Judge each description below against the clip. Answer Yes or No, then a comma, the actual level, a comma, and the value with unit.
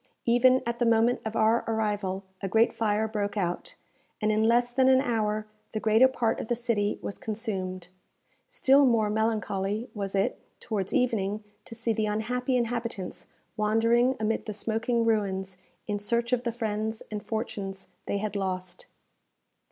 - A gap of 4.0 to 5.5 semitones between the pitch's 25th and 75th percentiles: No, narrow, 2.4 semitones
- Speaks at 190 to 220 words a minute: No, average, 160 wpm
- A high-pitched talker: Yes, high, 220 Hz